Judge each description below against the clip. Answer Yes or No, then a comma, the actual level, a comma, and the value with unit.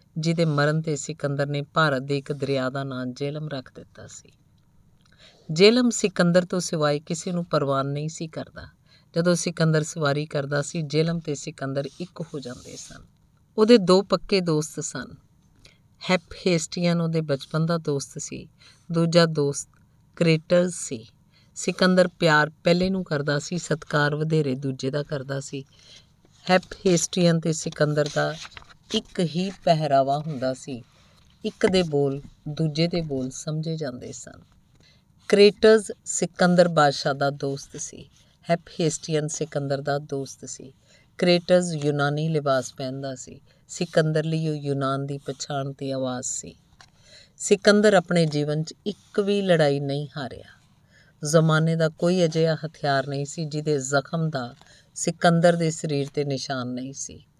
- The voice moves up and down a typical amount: Yes, average, 3.5 semitones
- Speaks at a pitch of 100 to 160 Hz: Yes, medium, 150 Hz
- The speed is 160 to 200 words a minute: No, average, 140 wpm